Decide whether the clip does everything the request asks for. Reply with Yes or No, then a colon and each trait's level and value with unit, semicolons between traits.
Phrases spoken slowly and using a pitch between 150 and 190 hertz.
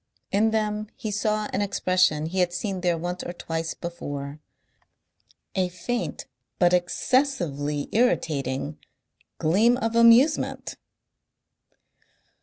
Yes: slow, 105 wpm; medium, 185 Hz